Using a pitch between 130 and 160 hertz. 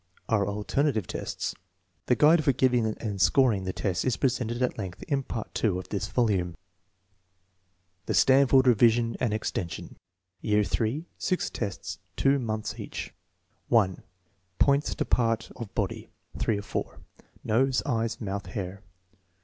No: low, 115 Hz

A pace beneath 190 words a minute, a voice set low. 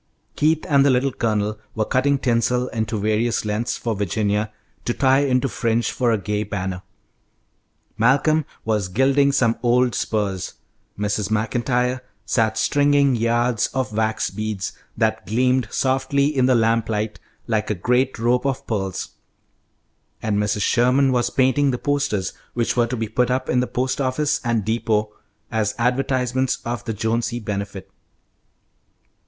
Yes: average, 145 wpm; low, 120 Hz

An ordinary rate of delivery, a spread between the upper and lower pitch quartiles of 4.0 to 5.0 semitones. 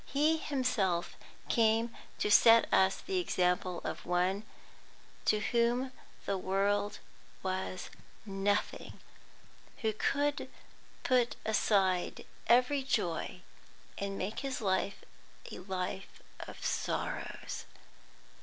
No: slow, 100 wpm; average, 4.5 semitones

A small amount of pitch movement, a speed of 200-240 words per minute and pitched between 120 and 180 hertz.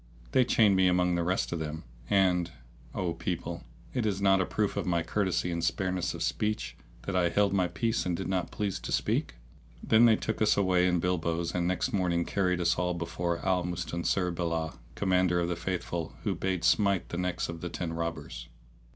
No: narrow, 2.0 semitones; fast, 205 wpm; very low, 90 Hz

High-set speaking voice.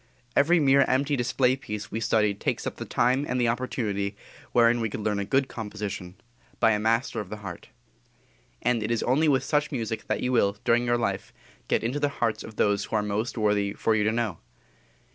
No: low, 115 Hz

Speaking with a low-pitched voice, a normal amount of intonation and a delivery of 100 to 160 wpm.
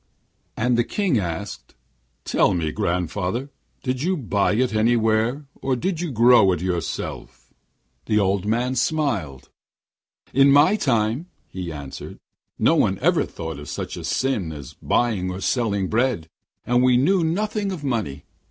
No: low, 115 Hz; wide, 6.4 semitones; average, 150 wpm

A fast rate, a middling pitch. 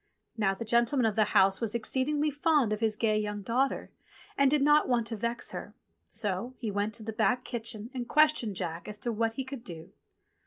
No: fast, 220 wpm; high, 230 Hz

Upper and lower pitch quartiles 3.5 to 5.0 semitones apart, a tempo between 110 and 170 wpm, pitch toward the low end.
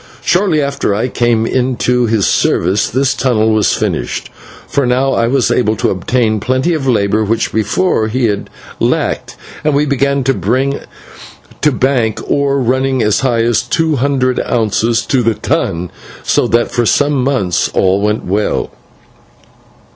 Yes: average, 3.9 semitones; average, 155 wpm; low, 125 Hz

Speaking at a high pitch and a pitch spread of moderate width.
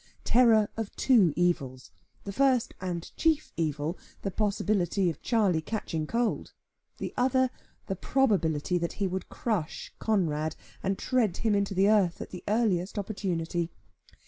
Yes: high, 195 Hz; average, 4.5 semitones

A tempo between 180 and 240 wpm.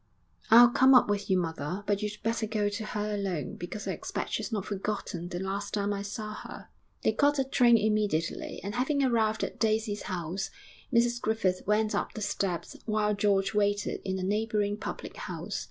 Yes: average, 190 wpm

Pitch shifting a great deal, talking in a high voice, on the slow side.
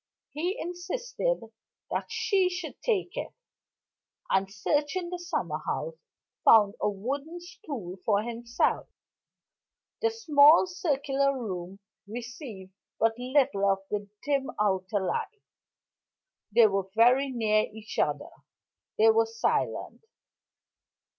Yes: wide, 9.0 semitones; very high, 270 Hz; slow, 110 wpm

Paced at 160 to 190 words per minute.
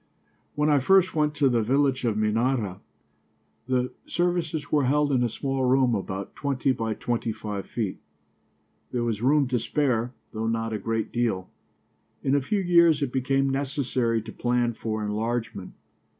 Yes: average, 165 wpm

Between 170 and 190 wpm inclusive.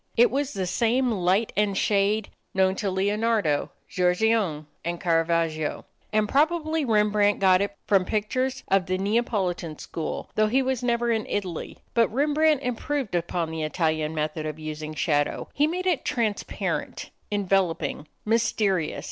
No: average, 145 wpm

